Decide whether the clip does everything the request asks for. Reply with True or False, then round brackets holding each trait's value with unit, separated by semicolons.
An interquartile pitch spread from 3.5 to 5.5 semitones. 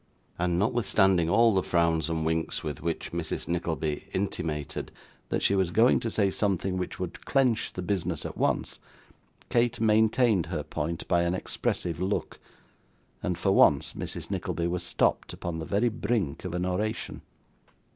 True (3.8 semitones)